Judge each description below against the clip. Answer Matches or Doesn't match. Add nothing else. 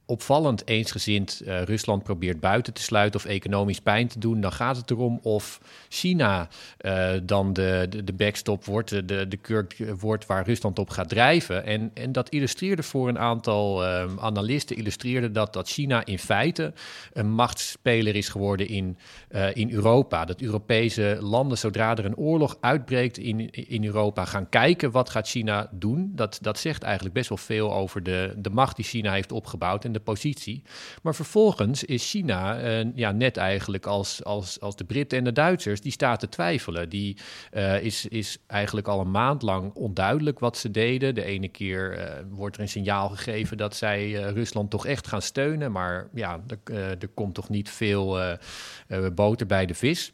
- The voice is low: Matches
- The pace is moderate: Matches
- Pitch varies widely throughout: Doesn't match